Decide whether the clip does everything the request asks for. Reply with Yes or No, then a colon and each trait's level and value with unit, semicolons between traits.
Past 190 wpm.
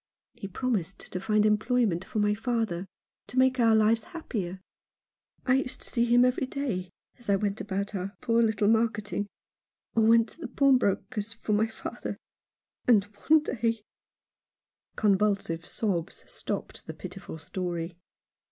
No: average, 155 wpm